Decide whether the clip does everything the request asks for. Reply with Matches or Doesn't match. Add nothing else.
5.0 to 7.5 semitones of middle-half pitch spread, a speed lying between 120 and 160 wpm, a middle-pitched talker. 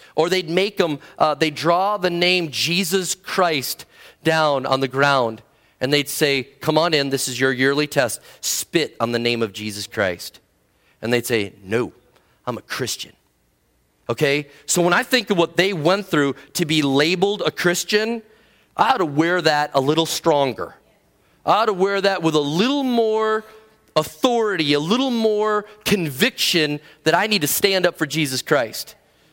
Doesn't match